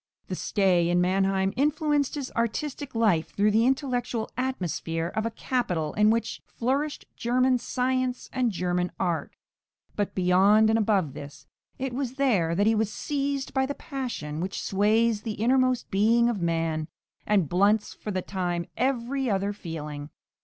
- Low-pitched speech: No, high, 215 Hz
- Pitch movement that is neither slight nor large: No, wide, 5.9 semitones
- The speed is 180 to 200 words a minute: No, average, 155 wpm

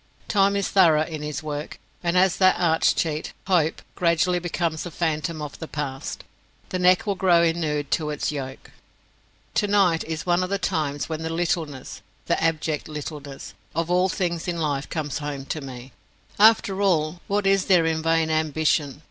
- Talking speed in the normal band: Yes, average, 175 wpm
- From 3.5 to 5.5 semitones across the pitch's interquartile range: No, average, 3.0 semitones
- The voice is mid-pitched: Yes, medium, 160 Hz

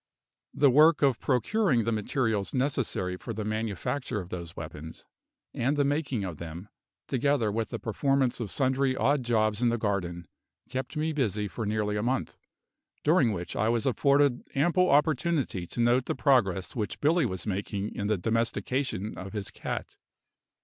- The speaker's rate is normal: Yes, average, 165 wpm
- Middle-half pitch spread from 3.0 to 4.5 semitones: No, average, 5.1 semitones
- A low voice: Yes, low, 115 Hz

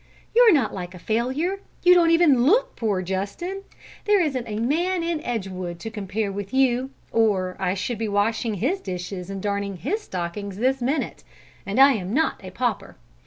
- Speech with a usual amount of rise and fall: No, wide, 7.4 semitones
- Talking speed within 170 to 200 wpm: Yes, average, 180 wpm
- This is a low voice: No, high, 225 Hz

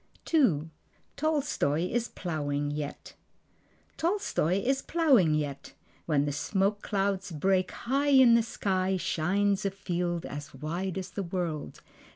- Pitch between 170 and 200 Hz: Yes, medium, 185 Hz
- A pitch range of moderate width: No, wide, 6.6 semitones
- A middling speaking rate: No, slow, 130 wpm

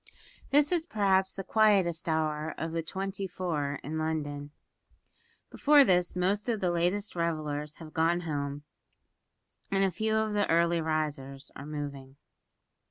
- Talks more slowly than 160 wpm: Yes, average, 140 wpm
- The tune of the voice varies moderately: Yes, average, 4.4 semitones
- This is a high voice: No, medium, 170 Hz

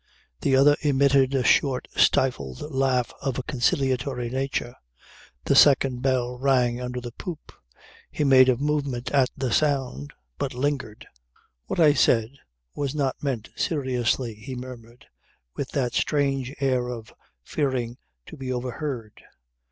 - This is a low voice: Yes, low, 130 Hz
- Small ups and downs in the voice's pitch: Yes, narrow, 2.1 semitones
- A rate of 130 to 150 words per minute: Yes, slow, 135 wpm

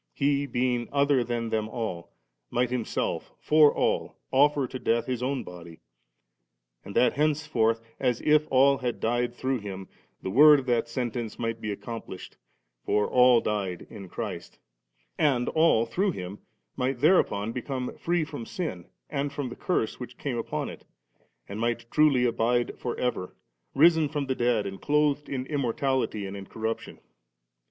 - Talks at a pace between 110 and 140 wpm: No, average, 160 wpm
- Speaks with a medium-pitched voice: No, low, 125 Hz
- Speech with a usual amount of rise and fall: Yes, average, 3.8 semitones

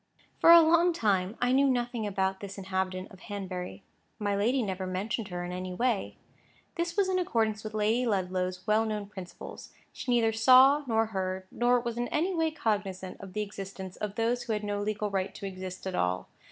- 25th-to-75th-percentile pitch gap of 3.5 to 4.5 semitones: Yes, average, 4.2 semitones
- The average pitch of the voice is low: No, high, 210 Hz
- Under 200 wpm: No, fast, 205 wpm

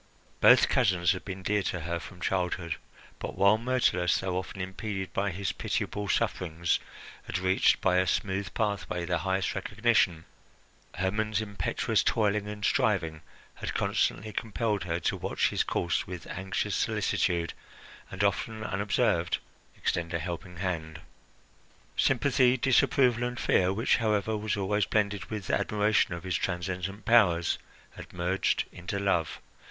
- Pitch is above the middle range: No, very low, 95 Hz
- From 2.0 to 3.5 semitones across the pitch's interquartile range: Yes, average, 3.1 semitones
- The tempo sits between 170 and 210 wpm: No, average, 140 wpm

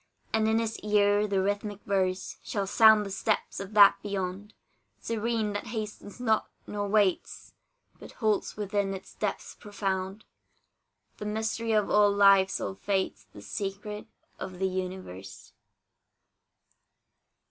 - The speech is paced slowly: Yes, slow, 130 wpm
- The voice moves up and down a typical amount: No, narrow, 1.7 semitones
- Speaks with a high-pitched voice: Yes, high, 205 Hz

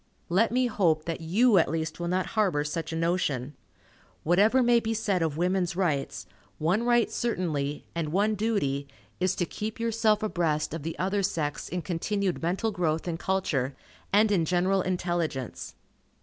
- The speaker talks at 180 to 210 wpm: No, average, 165 wpm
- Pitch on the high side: No, medium, 180 Hz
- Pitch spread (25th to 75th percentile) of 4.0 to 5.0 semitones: Yes, average, 4.5 semitones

